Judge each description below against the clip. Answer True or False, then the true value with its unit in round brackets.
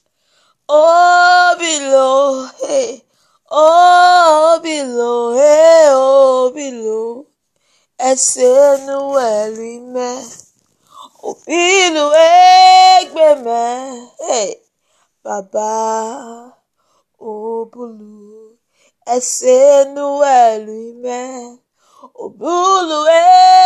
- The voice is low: False (275 Hz)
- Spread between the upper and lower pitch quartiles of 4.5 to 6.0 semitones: True (5.5 semitones)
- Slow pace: True (55 wpm)